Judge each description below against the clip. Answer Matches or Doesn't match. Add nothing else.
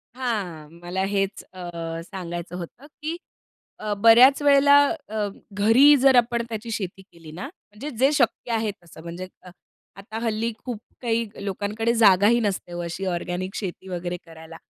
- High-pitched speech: Matches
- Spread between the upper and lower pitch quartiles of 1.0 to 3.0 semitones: Doesn't match